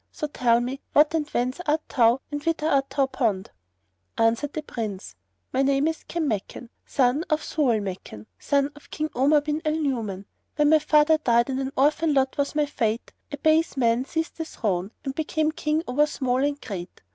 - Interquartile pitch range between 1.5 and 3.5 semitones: No, average, 4.2 semitones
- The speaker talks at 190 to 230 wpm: Yes, average, 195 wpm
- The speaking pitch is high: Yes, very high, 280 Hz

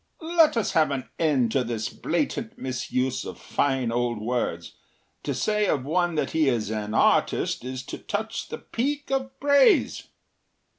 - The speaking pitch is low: No, medium, 145 Hz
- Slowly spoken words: No, average, 160 wpm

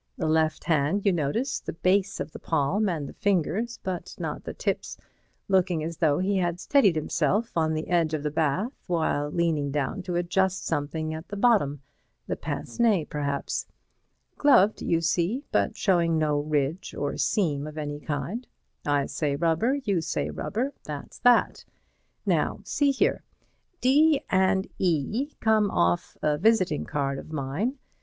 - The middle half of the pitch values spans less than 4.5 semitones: No, average, 5.2 semitones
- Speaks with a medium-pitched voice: Yes, medium, 170 Hz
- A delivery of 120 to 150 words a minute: No, average, 160 wpm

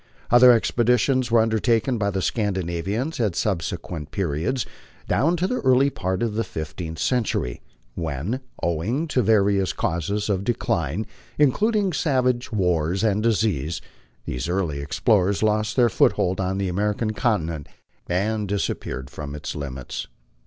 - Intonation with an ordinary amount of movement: No, wide, 5.7 semitones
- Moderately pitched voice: No, low, 100 Hz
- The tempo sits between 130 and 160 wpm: Yes, average, 140 wpm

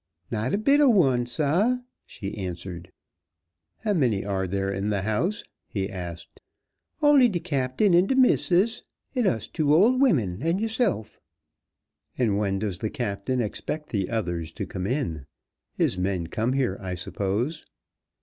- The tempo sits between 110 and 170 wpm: Yes, average, 155 wpm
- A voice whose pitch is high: No, low, 120 Hz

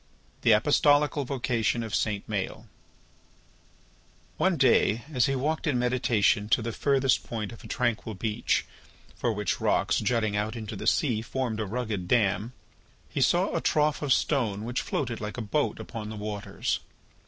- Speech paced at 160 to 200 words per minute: Yes, average, 165 wpm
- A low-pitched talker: Yes, low, 115 Hz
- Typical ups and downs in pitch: Yes, average, 3.6 semitones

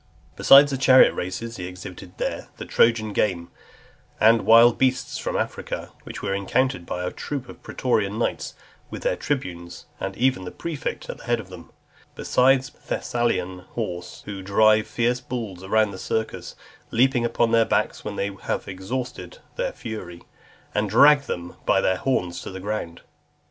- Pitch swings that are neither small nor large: Yes, average, 5.0 semitones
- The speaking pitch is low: Yes, low, 110 Hz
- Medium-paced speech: Yes, average, 165 wpm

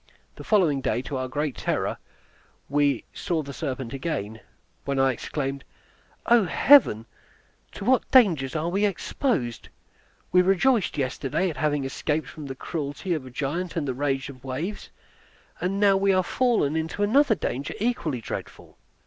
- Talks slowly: No, average, 155 wpm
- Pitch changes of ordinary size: No, wide, 6.1 semitones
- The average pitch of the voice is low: No, medium, 155 Hz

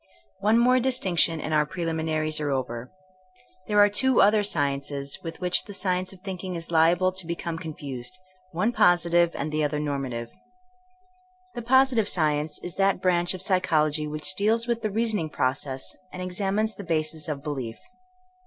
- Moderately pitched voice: Yes, medium, 170 Hz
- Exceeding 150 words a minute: Yes, average, 170 wpm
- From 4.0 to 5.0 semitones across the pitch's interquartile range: Yes, average, 4.7 semitones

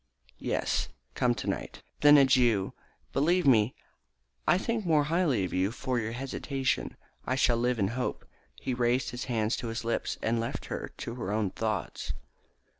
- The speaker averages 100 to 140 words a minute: No, average, 170 wpm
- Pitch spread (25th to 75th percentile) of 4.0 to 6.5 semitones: No, average, 3.2 semitones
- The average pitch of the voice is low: Yes, low, 125 Hz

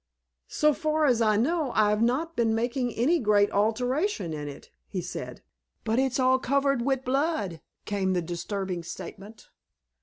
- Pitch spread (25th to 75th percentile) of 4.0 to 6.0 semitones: Yes, average, 5.0 semitones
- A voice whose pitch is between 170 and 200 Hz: No, high, 235 Hz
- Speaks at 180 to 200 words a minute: No, average, 155 wpm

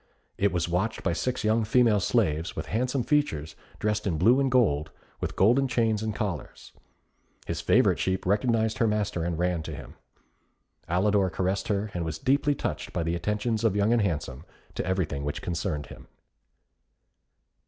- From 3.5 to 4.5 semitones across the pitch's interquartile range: No, average, 4.9 semitones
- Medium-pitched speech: No, low, 100 Hz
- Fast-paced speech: No, average, 170 wpm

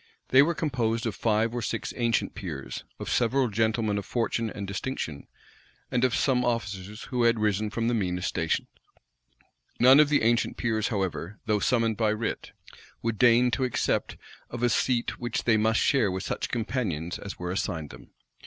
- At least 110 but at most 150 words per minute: No, average, 180 wpm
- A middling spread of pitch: Yes, average, 3.0 semitones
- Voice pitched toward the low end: Yes, low, 115 Hz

